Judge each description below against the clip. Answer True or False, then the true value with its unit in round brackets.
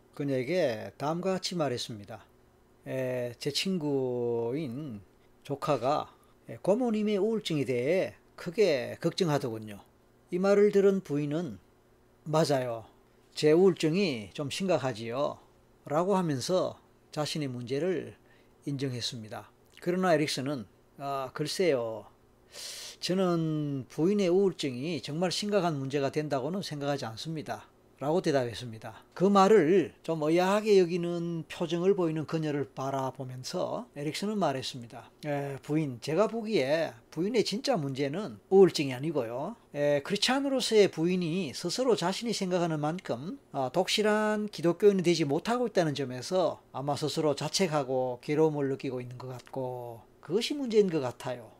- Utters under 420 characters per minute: True (300 characters per minute)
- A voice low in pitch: False (150 Hz)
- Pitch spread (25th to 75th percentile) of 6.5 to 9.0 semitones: False (5.9 semitones)